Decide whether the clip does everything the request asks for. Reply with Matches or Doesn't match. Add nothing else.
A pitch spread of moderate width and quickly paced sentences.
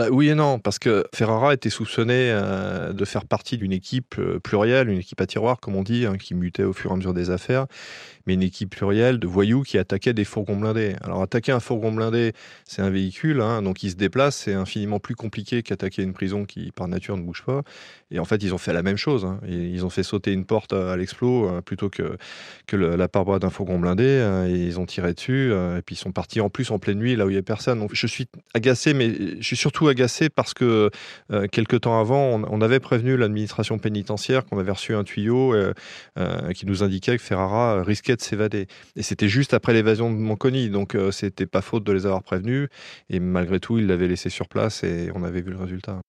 Matches